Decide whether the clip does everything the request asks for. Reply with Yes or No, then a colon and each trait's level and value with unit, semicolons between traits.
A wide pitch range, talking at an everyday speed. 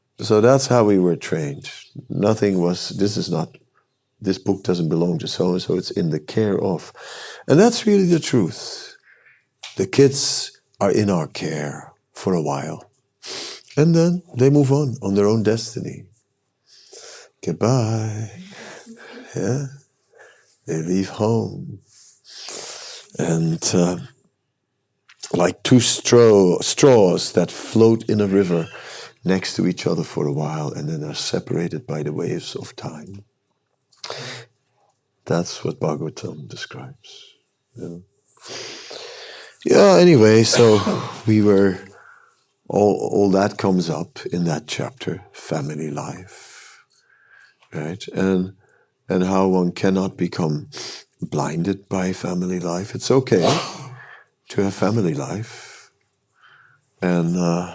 No: wide, 6.4 semitones; slow, 120 wpm